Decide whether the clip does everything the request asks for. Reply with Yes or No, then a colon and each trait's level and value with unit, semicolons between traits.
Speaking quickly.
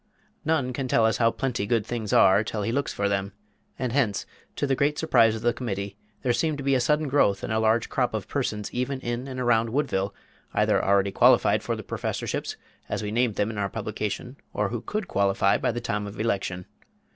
Yes: fast, 220 wpm